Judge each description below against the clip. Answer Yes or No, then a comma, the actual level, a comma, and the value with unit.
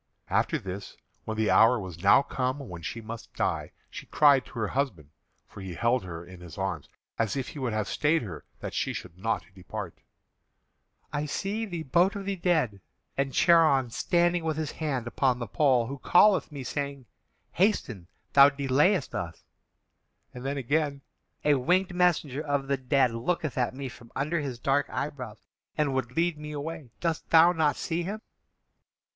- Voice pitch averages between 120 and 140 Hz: Yes, low, 135 Hz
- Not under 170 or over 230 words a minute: Yes, average, 180 wpm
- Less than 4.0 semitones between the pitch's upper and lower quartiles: No, wide, 5.4 semitones